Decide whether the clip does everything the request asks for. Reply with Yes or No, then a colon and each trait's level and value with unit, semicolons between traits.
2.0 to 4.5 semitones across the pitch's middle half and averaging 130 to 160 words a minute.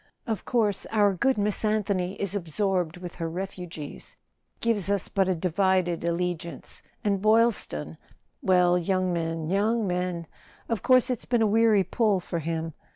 Yes: average, 3.4 semitones; average, 150 wpm